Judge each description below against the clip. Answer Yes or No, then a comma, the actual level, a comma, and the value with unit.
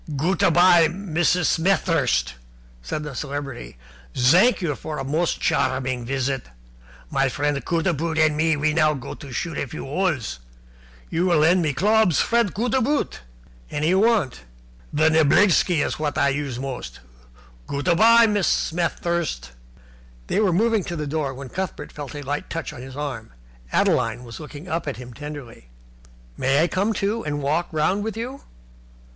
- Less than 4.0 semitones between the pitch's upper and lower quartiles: No, average, 4.6 semitones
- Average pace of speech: Yes, average, 170 wpm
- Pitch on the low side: No, medium, 155 Hz